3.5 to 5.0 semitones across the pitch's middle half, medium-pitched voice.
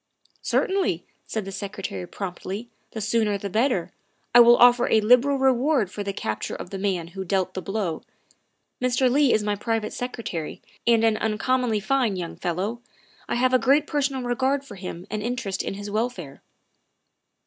No: average, 4.3 semitones; high, 220 Hz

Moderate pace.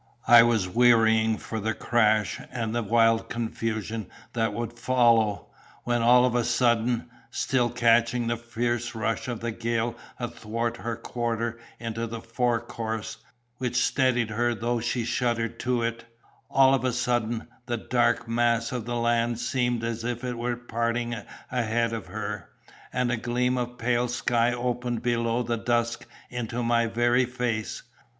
Yes: average, 155 wpm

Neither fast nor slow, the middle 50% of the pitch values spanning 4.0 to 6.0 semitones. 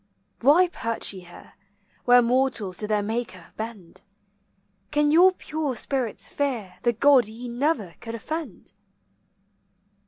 No: slow, 125 wpm; average, 4.9 semitones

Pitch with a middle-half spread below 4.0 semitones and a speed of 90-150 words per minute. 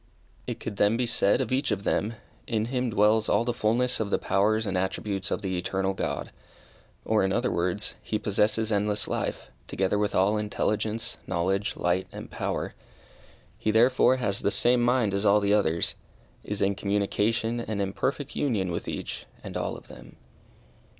No: average, 2.7 semitones; average, 180 wpm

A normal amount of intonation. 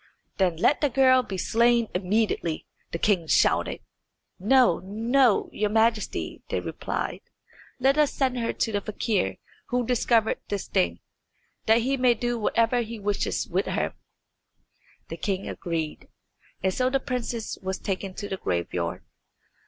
Yes: average, 4.4 semitones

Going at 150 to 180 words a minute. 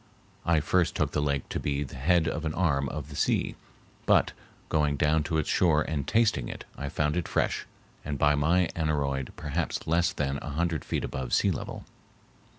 No: average, 195 wpm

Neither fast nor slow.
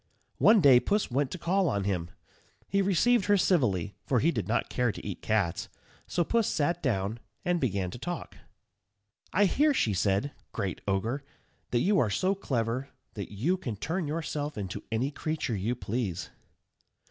Yes: average, 170 wpm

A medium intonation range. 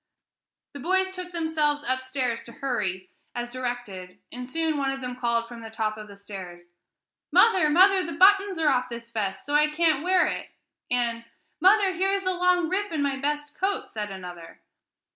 No: wide, 7.2 semitones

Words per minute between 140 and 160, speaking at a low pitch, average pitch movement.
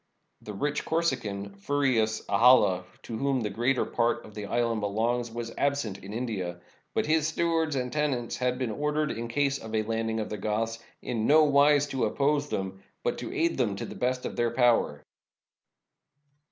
No: average, 180 wpm; low, 120 Hz; average, 4.5 semitones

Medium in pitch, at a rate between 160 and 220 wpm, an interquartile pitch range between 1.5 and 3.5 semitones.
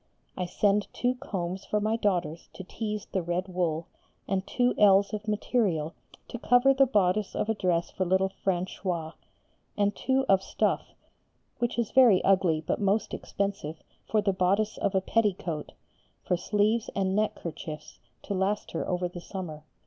No: high, 195 Hz; average, 165 wpm; average, 3.0 semitones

